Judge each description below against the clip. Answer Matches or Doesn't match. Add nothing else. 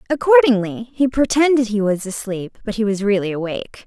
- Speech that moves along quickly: Doesn't match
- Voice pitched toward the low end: Doesn't match